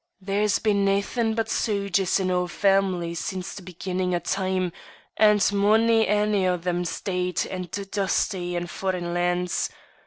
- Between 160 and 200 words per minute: No, average, 150 wpm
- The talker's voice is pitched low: No, high, 190 Hz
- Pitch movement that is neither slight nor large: No, narrow, 2.2 semitones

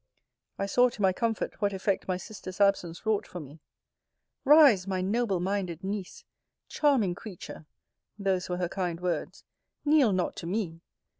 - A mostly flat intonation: No, average, 3.2 semitones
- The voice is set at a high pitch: Yes, high, 195 Hz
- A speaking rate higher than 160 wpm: No, average, 155 wpm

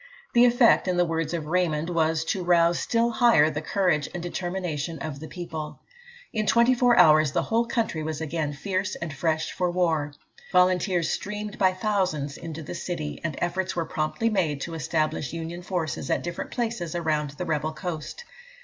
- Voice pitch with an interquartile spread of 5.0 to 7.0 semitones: No, average, 3.2 semitones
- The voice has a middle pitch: Yes, medium, 170 Hz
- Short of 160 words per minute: No, average, 180 wpm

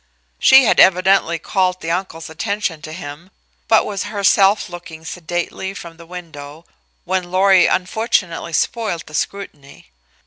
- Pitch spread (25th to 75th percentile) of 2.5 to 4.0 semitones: Yes, average, 2.9 semitones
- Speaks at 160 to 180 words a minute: No, slow, 135 wpm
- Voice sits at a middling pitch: Yes, medium, 180 Hz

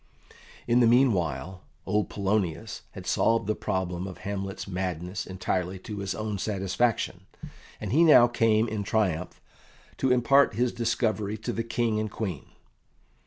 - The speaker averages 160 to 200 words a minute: No, average, 145 wpm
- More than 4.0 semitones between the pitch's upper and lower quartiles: No, average, 3.6 semitones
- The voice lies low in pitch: Yes, low, 105 Hz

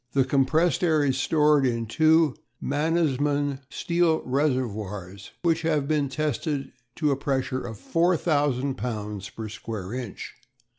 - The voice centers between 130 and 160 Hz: Yes, medium, 140 Hz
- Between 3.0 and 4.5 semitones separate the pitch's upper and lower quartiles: Yes, average, 3.9 semitones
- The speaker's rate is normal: No, slow, 130 wpm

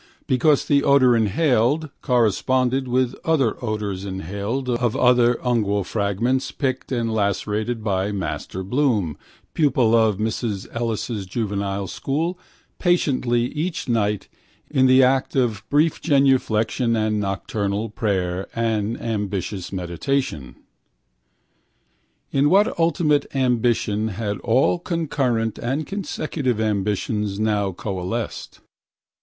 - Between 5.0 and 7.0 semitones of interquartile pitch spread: No, average, 4.3 semitones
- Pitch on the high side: No, low, 115 Hz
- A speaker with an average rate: No, slow, 105 wpm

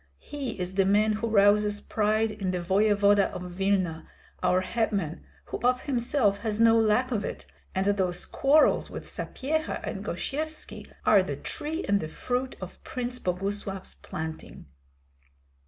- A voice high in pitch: Yes, high, 210 Hz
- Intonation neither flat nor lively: Yes, average, 4.1 semitones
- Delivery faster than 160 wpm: No, average, 150 wpm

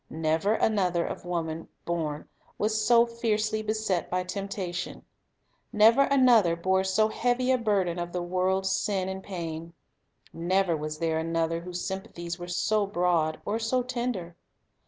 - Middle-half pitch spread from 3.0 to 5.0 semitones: Yes, average, 4.2 semitones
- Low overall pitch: No, high, 190 Hz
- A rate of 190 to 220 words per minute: No, average, 145 wpm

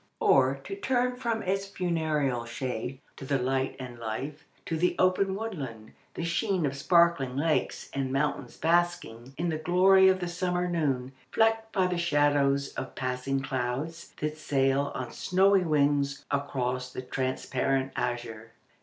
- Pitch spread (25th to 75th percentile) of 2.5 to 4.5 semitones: No, average, 5.3 semitones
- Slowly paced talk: No, average, 150 wpm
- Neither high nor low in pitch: Yes, medium, 145 Hz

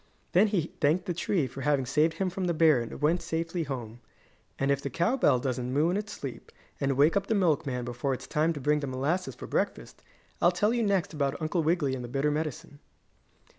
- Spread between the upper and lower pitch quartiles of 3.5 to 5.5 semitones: Yes, average, 4.3 semitones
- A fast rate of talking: Yes, fast, 225 wpm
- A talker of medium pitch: Yes, medium, 150 Hz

